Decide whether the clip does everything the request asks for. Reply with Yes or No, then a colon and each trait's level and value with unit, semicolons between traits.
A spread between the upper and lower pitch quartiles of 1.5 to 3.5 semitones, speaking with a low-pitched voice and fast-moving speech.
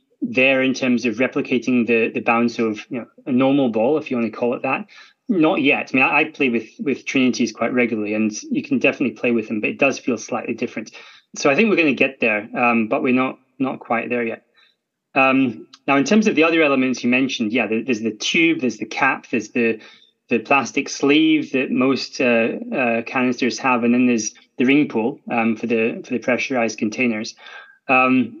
Yes: average, 2.8 semitones; low, 125 Hz; fast, 220 wpm